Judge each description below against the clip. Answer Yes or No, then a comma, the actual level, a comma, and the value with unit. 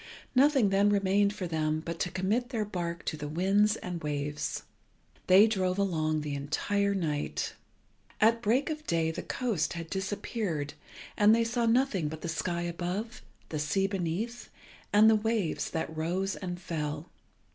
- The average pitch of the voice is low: No, medium, 185 Hz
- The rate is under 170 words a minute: Yes, average, 160 wpm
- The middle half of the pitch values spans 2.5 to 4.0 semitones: No, average, 4.8 semitones